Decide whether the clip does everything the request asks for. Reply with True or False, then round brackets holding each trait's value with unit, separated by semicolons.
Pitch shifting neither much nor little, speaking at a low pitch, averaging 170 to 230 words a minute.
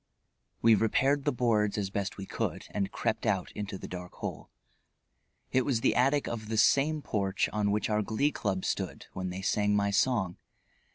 True (3.9 semitones; 105 Hz; 185 wpm)